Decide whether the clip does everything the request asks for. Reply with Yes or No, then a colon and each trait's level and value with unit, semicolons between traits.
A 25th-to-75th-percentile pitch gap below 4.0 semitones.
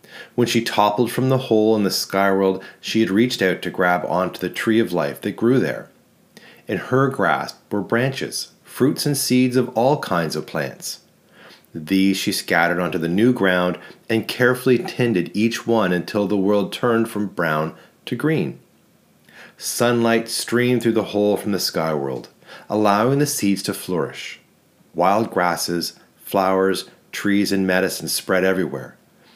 No: average, 4.3 semitones